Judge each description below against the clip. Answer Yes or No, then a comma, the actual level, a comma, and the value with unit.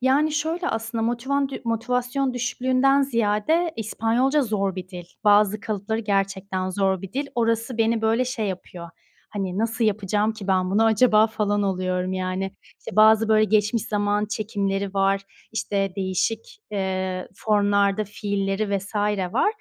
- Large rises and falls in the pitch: No, average, 2.9 semitones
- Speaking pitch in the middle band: No, high, 215 Hz